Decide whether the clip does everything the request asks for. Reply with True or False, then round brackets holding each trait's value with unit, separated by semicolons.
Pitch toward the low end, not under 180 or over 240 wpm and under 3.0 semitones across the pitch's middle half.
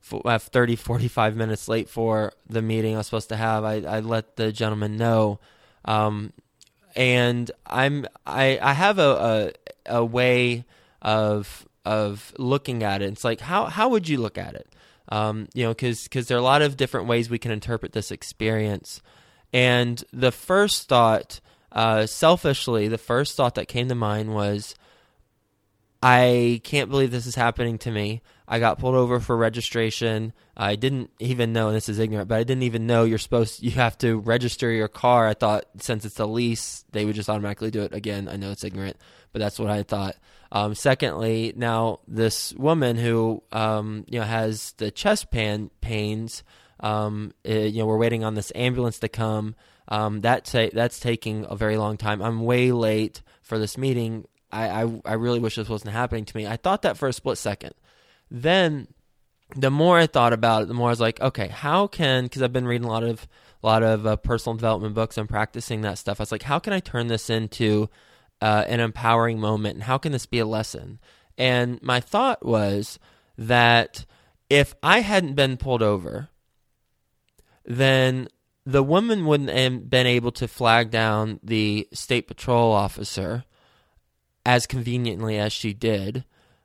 True (115 Hz; 190 wpm; 2.4 semitones)